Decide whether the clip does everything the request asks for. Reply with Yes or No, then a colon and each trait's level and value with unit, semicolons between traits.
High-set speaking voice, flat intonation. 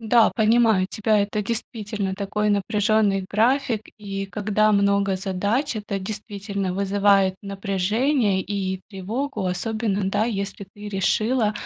Yes: high, 205 Hz; narrow, 1.8 semitones